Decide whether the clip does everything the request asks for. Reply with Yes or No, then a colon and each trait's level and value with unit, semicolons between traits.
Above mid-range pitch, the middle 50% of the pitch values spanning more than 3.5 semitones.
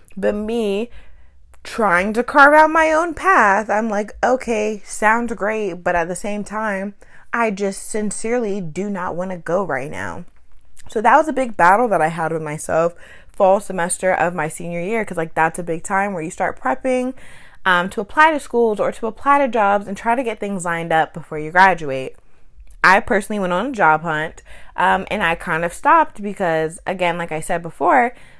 Yes: high, 195 Hz; average, 4.9 semitones